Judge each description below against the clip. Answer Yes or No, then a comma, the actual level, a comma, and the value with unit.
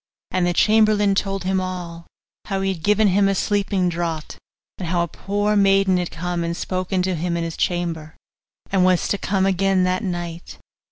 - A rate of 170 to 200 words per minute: Yes, average, 190 wpm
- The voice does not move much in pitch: Yes, narrow, 2.1 semitones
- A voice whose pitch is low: No, medium, 185 Hz